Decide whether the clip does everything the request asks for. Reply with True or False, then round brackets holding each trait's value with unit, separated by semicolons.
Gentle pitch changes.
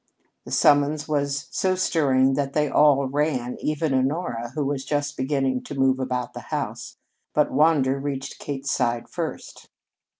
True (2.0 semitones)